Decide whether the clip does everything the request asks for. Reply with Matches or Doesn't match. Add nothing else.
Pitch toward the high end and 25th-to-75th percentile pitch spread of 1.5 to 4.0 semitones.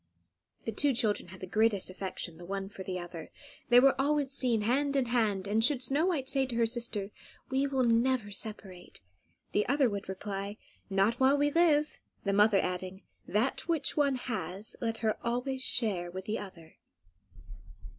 Doesn't match